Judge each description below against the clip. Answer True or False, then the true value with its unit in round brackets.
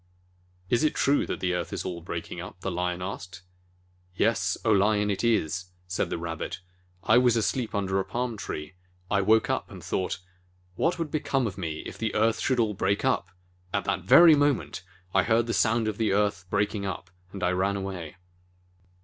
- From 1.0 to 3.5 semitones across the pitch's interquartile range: False (4.1 semitones)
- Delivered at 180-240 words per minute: True (200 wpm)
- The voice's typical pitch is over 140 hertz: False (100 Hz)